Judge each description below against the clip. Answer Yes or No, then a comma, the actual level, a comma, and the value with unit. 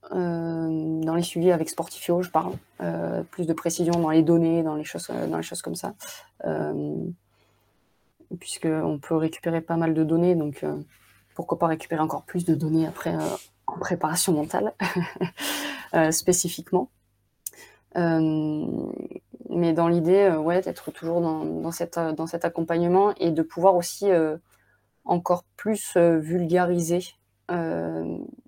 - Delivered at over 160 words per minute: No, average, 150 wpm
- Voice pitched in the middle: Yes, medium, 165 Hz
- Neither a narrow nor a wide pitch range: No, narrow, 1.9 semitones